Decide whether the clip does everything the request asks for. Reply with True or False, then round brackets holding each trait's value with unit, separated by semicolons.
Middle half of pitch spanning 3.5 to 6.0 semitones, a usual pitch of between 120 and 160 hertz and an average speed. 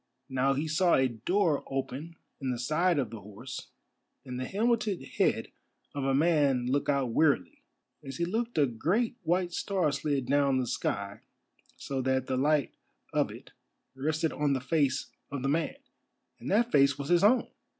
True (4.4 semitones; 140 Hz; 175 wpm)